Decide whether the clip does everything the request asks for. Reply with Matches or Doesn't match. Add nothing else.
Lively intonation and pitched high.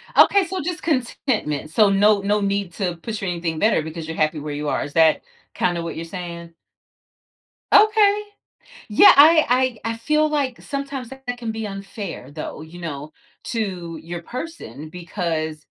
Matches